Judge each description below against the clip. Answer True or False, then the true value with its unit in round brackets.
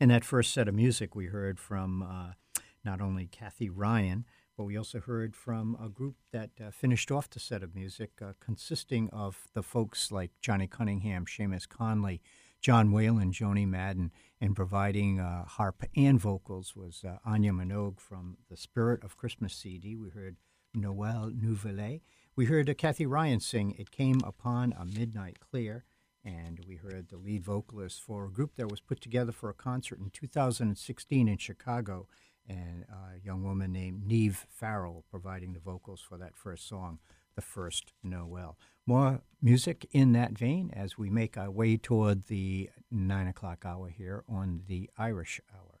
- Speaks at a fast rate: False (175 wpm)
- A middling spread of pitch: True (3.8 semitones)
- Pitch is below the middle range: True (105 Hz)